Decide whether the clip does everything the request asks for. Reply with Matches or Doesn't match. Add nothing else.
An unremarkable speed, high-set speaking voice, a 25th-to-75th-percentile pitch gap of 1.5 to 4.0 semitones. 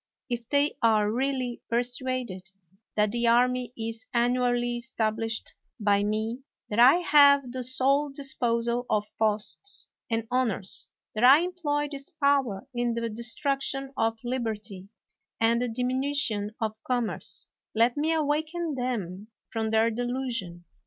Doesn't match